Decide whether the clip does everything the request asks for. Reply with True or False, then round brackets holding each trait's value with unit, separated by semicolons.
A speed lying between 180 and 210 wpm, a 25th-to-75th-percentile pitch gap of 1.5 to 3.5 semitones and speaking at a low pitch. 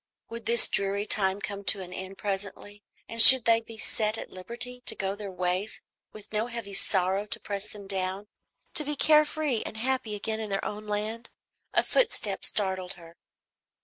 False (185 wpm; 2.8 semitones; 210 Hz)